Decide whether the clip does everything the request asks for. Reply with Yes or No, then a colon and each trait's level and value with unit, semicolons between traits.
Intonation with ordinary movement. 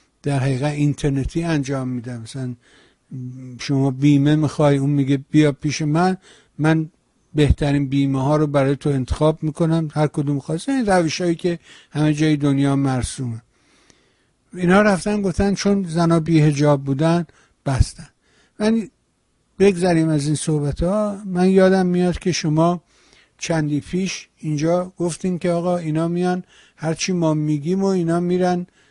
Yes: average, 3.8 semitones